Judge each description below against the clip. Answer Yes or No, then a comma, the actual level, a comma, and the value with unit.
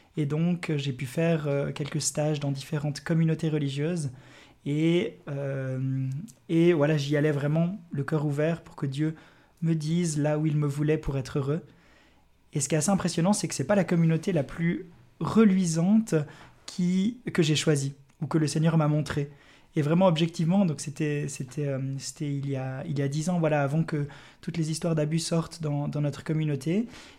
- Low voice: No, medium, 155 Hz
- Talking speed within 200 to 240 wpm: No, average, 190 wpm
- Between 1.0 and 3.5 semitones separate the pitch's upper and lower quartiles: Yes, narrow, 2.5 semitones